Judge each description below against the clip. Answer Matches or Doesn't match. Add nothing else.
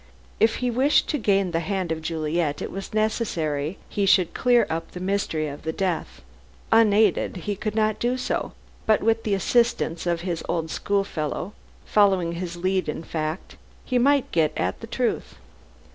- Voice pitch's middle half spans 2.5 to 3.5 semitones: Doesn't match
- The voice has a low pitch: Doesn't match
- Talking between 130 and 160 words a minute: Doesn't match